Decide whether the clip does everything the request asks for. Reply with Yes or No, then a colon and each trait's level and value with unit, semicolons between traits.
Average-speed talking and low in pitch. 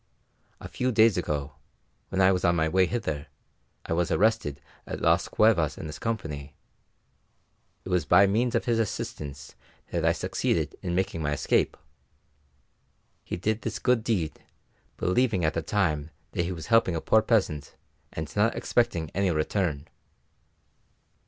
Yes: average, 155 wpm; very low, 90 Hz